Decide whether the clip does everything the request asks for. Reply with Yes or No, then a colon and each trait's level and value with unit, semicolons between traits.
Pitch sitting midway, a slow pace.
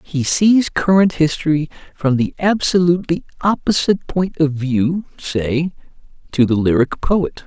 Yes: medium, 160 Hz; slow, 130 wpm